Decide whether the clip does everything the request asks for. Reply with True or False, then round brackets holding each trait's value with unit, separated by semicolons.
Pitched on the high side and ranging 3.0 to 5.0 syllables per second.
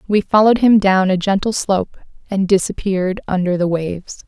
False (195 Hz; 5.6 syllables/s)